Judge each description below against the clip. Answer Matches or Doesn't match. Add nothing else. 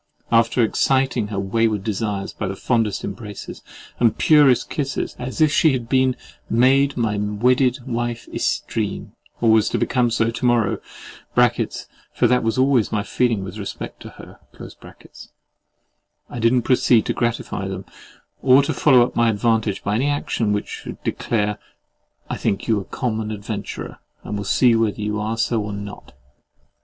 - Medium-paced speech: Matches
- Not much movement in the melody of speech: Doesn't match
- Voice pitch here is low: Matches